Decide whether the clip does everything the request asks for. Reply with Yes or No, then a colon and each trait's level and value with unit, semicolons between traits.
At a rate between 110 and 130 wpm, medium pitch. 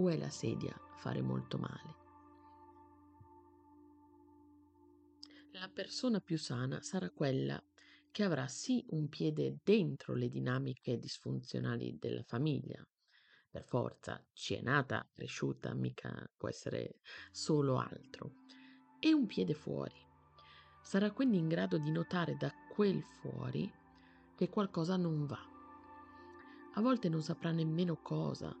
Yes: slow, 115 wpm; medium, 180 Hz